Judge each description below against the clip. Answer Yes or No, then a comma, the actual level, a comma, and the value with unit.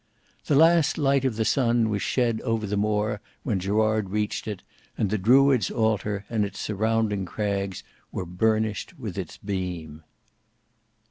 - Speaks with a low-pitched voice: Yes, low, 105 Hz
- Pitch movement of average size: No, narrow, 2.3 semitones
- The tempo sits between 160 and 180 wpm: No, average, 150 wpm